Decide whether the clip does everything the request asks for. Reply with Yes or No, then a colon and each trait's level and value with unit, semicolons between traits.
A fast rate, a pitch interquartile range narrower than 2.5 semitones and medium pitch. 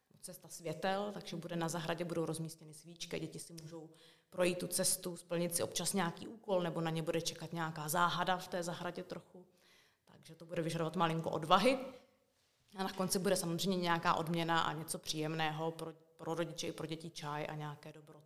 Yes: fast, 185 wpm; narrow, 2.0 semitones; medium, 170 Hz